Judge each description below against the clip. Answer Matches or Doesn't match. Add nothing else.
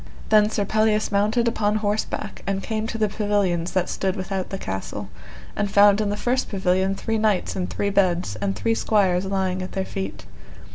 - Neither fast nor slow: Matches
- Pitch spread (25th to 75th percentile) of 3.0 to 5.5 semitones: Doesn't match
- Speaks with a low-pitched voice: Doesn't match